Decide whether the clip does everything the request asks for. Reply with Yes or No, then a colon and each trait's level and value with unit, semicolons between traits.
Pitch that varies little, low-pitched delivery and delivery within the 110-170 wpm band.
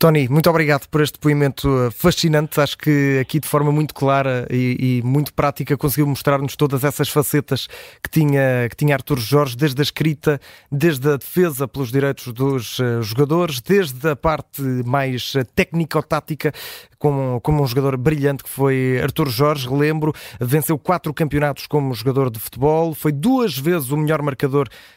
No: narrow, 2.3 semitones; medium, 145 Hz; average, 165 wpm